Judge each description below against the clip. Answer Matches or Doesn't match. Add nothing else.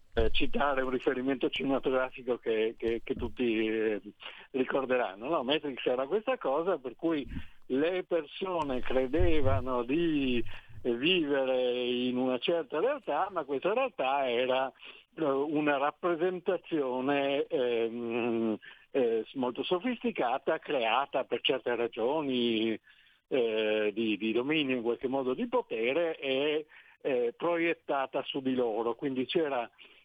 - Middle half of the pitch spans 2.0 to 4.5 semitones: Doesn't match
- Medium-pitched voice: Doesn't match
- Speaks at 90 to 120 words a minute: Matches